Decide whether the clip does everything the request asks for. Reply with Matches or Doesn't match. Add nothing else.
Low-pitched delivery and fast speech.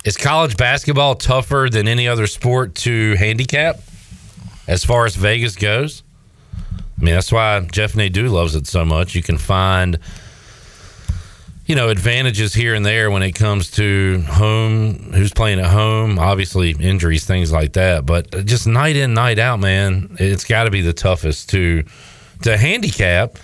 Doesn't match